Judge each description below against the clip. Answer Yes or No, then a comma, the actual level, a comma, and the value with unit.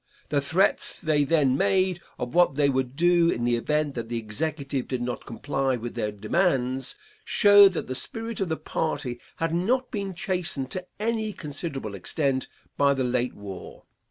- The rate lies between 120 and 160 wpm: No, average, 175 wpm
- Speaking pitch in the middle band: Yes, medium, 145 Hz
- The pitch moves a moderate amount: No, wide, 5.9 semitones